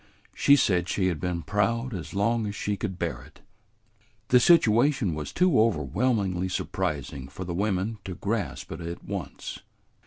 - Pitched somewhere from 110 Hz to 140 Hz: No, low, 100 Hz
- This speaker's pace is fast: No, average, 160 wpm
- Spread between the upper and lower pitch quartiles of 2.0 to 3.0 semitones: No, average, 4.7 semitones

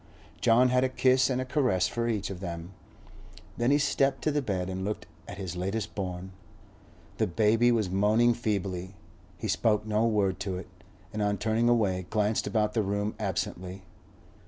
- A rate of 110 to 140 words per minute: No, average, 180 wpm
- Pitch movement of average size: Yes, average, 3.8 semitones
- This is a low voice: Yes, low, 105 Hz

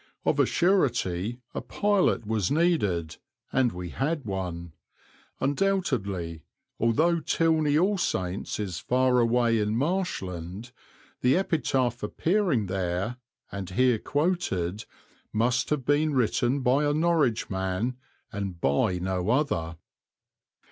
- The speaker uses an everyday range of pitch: No, wide, 7.9 semitones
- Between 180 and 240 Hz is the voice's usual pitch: No, low, 120 Hz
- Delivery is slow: Yes, slow, 115 wpm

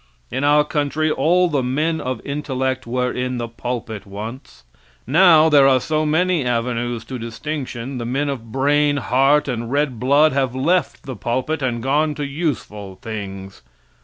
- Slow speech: No, average, 160 wpm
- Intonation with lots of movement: No, average, 3.7 semitones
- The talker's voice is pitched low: Yes, low, 130 Hz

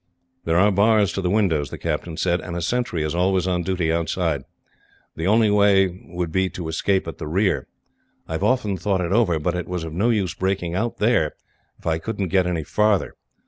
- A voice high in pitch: No, very low, 90 Hz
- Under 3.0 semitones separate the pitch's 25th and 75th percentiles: No, average, 3.3 semitones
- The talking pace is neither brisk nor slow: No, fast, 220 wpm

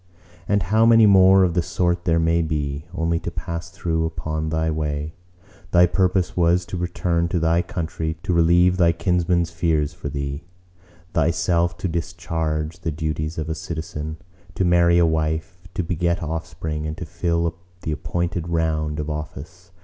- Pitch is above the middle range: No, very low, 85 Hz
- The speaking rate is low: No, average, 165 wpm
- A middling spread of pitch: No, narrow, 1.9 semitones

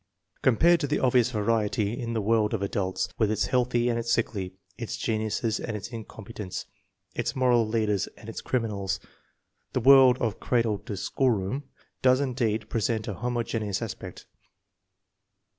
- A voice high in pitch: No, low, 115 Hz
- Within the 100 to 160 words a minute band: Yes, average, 150 wpm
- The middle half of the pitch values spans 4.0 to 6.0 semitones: No, average, 2.8 semitones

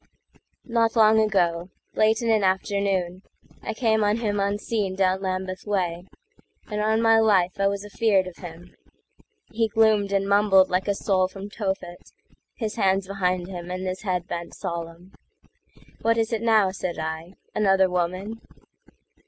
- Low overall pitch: No, high, 195 Hz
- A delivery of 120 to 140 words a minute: Yes, slow, 135 wpm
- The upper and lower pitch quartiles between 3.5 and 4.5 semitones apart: No, average, 2.7 semitones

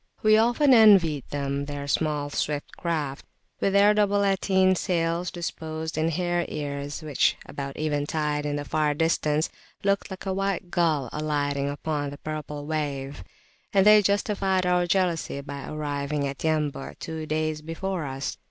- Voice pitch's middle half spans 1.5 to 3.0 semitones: No, average, 4.3 semitones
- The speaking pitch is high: No, medium, 155 Hz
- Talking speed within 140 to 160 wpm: Yes, average, 150 wpm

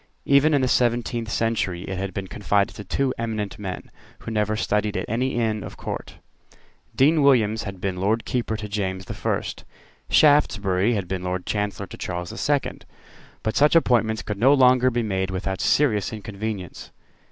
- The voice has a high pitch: No, low, 105 Hz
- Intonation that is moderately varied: Yes, average, 3.9 semitones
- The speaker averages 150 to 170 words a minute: No, average, 180 wpm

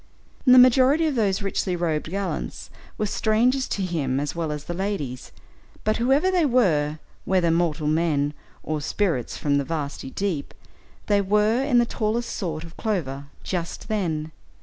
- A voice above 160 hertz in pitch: Yes, medium, 185 Hz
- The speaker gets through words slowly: No, average, 160 wpm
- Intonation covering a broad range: Yes, wide, 6.3 semitones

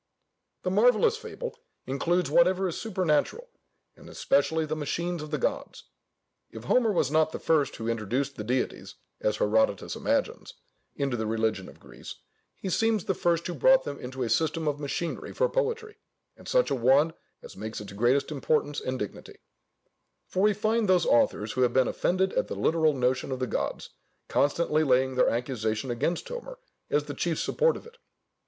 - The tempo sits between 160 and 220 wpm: Yes, average, 180 wpm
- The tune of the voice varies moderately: No, wide, 7.0 semitones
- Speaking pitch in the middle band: Yes, medium, 155 Hz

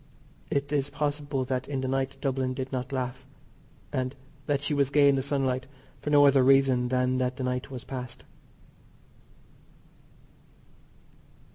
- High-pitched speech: No, low, 135 Hz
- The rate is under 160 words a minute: Yes, average, 150 wpm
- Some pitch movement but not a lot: No, narrow, 1.6 semitones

